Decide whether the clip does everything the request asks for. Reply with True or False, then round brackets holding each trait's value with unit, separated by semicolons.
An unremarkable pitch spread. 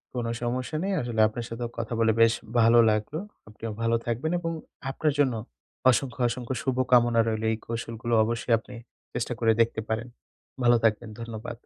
False (1.7 semitones)